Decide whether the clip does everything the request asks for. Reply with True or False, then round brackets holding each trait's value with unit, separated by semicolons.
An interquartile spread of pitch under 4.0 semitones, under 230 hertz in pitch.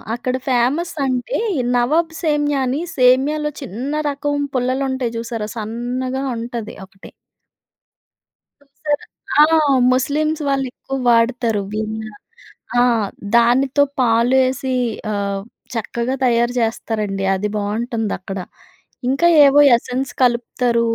False (3.0 semitones; 250 Hz)